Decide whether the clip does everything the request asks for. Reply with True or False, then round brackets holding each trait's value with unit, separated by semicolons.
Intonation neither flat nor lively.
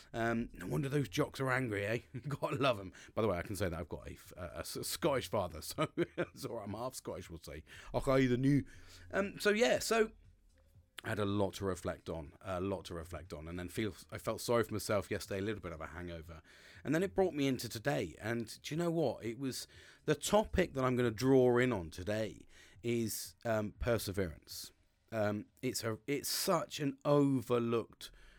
False (6.2 semitones)